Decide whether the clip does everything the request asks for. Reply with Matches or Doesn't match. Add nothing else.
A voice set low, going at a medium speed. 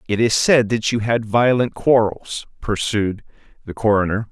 Matches